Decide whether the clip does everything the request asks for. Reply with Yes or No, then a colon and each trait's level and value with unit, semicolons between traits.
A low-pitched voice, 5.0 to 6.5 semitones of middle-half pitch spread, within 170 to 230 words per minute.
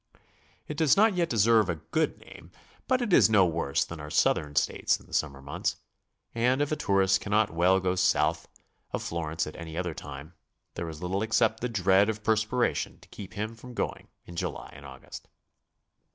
Yes: very low, 95 Hz; wide, 5.4 semitones; average, 195 wpm